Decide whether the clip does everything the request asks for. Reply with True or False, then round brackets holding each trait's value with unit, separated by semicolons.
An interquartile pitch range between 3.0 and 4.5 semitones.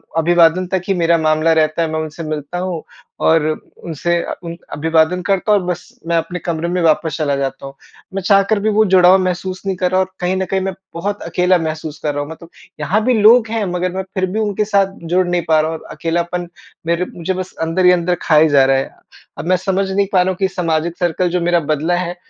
False (2.5 semitones)